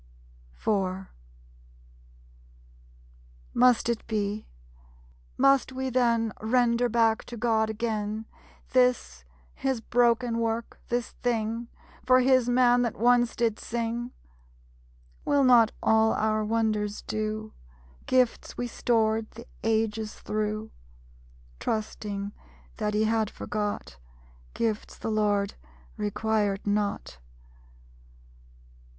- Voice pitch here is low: No, high, 225 Hz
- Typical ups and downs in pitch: No, narrow, 2.0 semitones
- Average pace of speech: No, slow, 100 wpm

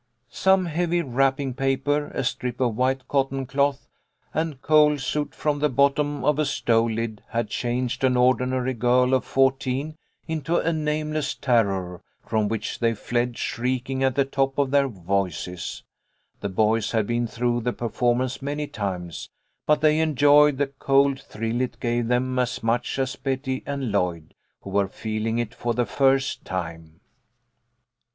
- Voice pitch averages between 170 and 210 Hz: No, low, 130 Hz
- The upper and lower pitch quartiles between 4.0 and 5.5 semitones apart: No, average, 3.4 semitones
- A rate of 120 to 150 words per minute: No, average, 160 wpm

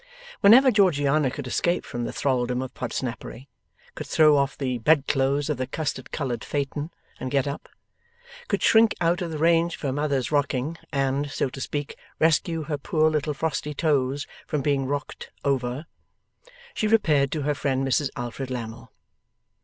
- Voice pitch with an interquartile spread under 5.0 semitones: Yes, average, 2.9 semitones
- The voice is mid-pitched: Yes, medium, 145 Hz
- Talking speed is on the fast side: No, average, 165 wpm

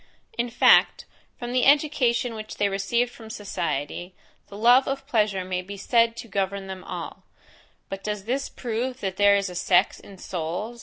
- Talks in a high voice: Yes, high, 210 Hz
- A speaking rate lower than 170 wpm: No, average, 175 wpm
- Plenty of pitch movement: No, average, 3.8 semitones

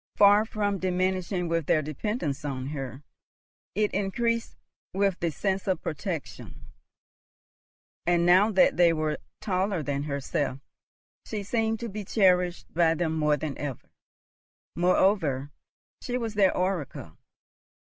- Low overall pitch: No, medium, 180 Hz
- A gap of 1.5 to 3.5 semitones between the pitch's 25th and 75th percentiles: No, average, 4.8 semitones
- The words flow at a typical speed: No, slow, 130 wpm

